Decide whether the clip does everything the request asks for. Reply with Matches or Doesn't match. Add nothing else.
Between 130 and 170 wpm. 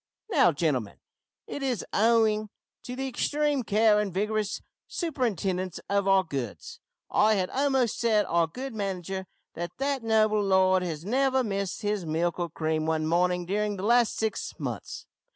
Matches